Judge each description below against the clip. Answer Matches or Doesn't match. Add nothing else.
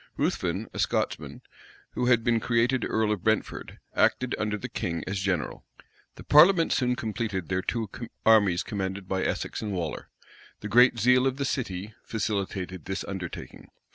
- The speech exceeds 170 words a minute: Doesn't match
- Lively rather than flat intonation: Doesn't match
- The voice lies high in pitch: Doesn't match